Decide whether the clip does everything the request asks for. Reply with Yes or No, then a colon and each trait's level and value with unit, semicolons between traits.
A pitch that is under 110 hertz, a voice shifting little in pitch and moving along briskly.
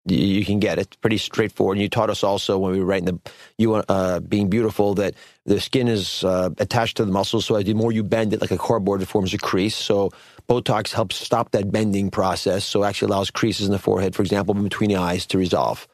Yes: low, 100 Hz; narrow, 2.2 semitones; fast, 250 wpm